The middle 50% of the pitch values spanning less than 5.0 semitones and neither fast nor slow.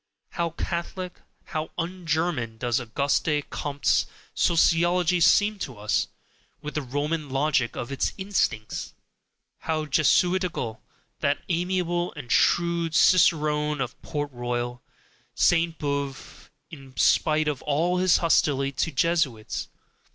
No: average, 4.0 semitones; slow, 115 wpm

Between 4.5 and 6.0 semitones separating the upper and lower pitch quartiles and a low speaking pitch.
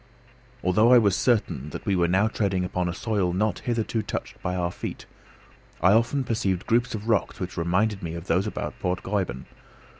No: average, 3.5 semitones; very low, 95 Hz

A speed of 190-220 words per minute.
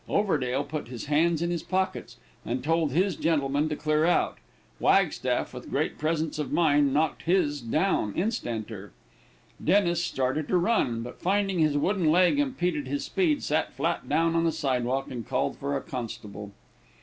No: average, 165 wpm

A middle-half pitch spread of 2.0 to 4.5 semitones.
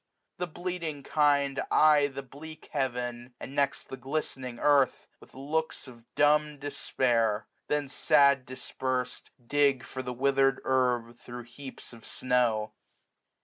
Yes: average, 2.8 semitones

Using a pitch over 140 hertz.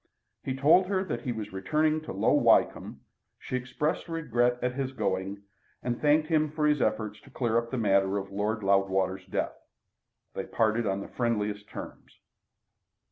No: low, 115 Hz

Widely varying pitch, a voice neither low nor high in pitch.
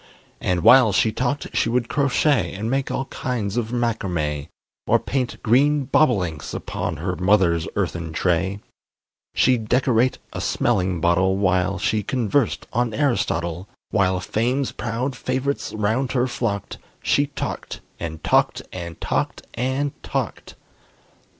No: wide, 5.8 semitones; low, 110 Hz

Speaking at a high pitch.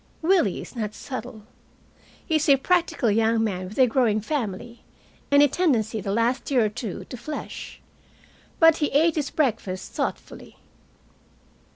Yes: high, 245 Hz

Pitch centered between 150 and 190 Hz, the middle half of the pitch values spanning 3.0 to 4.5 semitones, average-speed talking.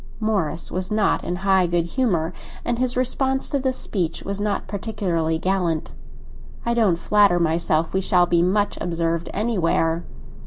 Yes: medium, 185 Hz; average, 4.1 semitones; average, 155 wpm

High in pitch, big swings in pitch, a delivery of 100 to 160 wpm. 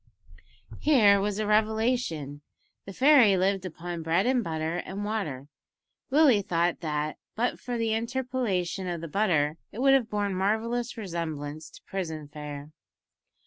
Yes: high, 195 Hz; wide, 5.7 semitones; average, 145 wpm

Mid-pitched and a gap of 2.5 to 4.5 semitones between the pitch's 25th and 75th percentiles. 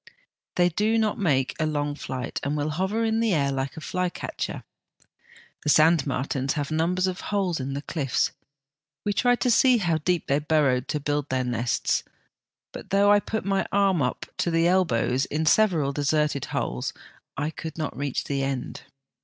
No: medium, 155 Hz; average, 5.1 semitones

